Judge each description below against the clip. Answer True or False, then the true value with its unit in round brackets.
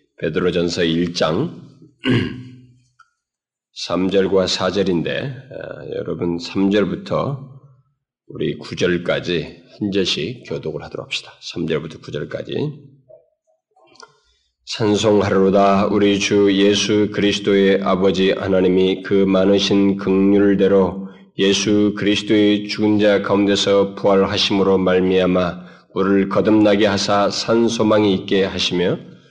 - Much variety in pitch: False (1.6 semitones)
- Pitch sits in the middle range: False (100 Hz)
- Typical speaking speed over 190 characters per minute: True (230 characters per minute)